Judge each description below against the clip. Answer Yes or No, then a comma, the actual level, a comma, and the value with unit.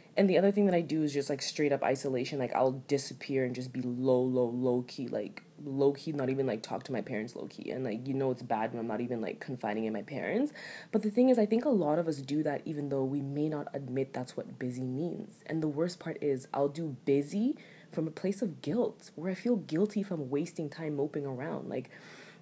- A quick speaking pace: Yes, fast, 255 wpm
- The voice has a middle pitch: Yes, medium, 145 Hz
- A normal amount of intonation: Yes, average, 4.4 semitones